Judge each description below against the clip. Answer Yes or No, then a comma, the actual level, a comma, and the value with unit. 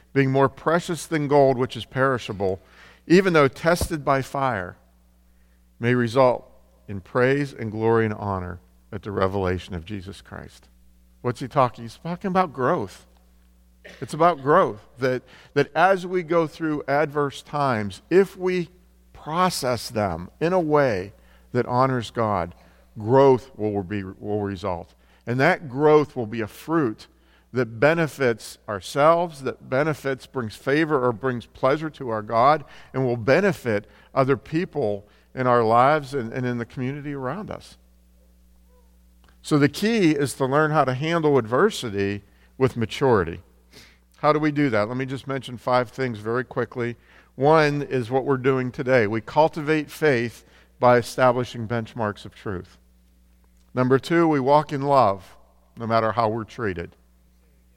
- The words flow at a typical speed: Yes, average, 150 wpm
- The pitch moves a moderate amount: No, wide, 6.5 semitones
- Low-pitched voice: Yes, low, 125 Hz